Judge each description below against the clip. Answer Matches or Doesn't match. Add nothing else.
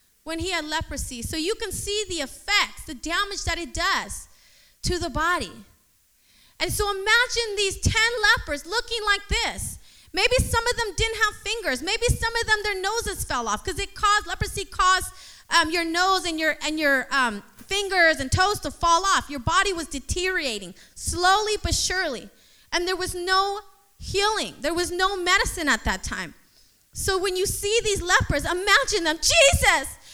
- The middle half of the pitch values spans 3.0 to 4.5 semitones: Matches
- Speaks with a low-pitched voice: Doesn't match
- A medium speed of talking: Matches